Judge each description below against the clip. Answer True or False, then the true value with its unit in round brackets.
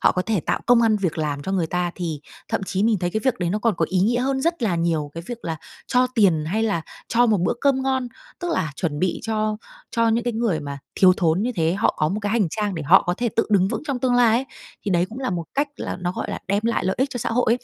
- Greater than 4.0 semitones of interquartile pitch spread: True (5.2 semitones)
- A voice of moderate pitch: False (205 Hz)